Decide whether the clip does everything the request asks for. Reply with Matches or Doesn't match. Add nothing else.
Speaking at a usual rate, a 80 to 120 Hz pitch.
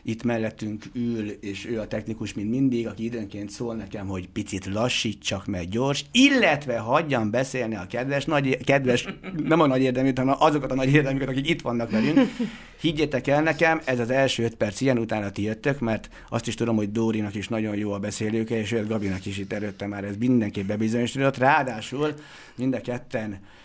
Doesn't match